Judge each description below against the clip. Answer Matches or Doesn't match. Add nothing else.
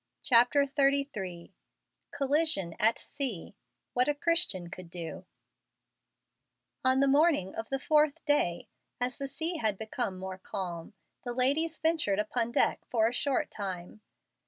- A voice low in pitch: Doesn't match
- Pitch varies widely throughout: Matches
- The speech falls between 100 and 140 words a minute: Matches